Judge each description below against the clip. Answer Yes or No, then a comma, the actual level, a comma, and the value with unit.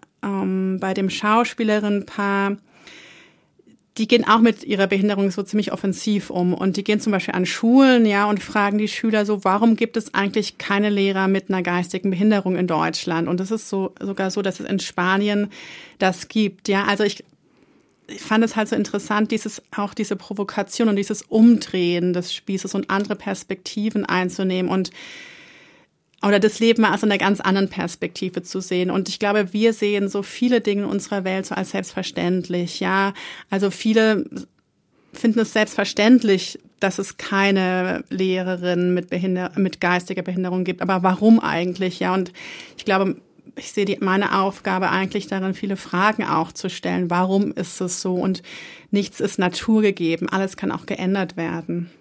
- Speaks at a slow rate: No, average, 170 wpm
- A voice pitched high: Yes, high, 195 Hz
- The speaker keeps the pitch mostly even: Yes, narrow, 2.1 semitones